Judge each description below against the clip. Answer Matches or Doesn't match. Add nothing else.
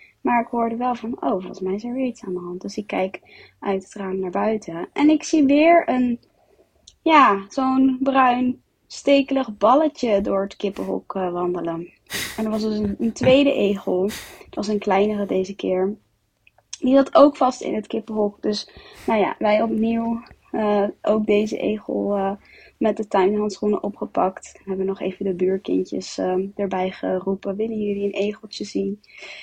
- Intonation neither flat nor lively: Matches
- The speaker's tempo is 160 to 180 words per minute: Matches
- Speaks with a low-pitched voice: Doesn't match